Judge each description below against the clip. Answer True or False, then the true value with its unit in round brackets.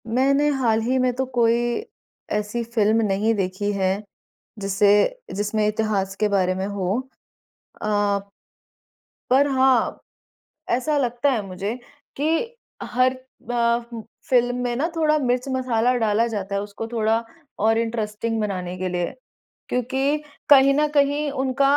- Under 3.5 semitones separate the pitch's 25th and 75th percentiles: False (4.2 semitones)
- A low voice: False (230 Hz)